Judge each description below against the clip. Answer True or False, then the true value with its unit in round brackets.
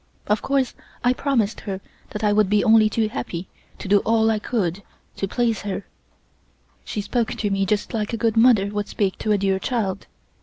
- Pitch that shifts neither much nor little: False (2.3 semitones)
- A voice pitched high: True (210 Hz)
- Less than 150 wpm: False (200 wpm)